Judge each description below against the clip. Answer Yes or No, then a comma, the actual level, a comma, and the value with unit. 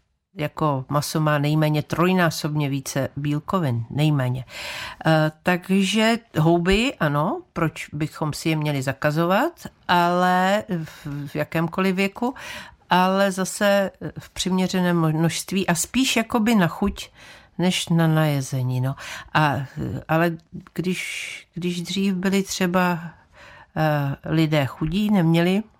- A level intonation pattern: No, average, 3.9 semitones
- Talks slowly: Yes, slow, 105 wpm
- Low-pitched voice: No, medium, 170 Hz